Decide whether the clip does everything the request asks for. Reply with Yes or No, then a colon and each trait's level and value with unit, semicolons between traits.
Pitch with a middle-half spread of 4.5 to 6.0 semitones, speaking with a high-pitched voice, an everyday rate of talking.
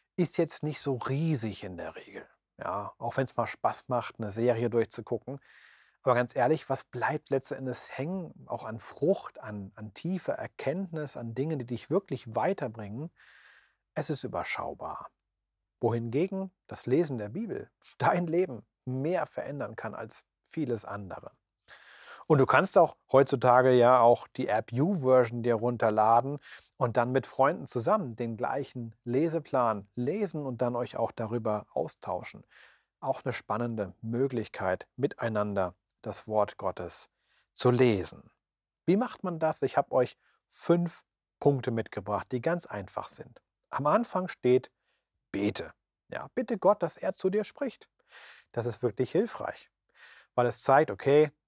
No: average, 4.8 semitones; low, 125 Hz; average, 145 wpm